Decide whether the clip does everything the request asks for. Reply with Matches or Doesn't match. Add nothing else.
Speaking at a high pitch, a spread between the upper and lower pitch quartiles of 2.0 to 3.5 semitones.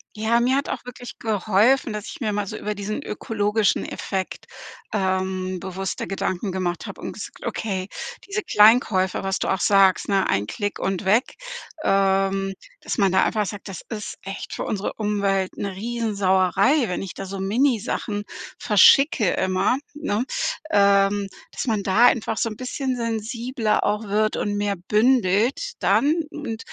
Matches